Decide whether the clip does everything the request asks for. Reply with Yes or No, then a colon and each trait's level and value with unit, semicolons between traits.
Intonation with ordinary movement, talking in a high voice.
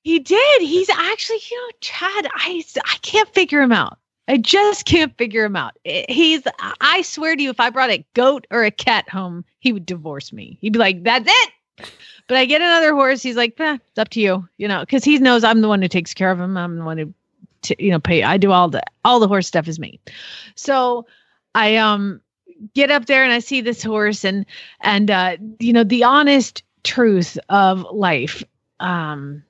No: wide, 7.0 semitones; high, 235 Hz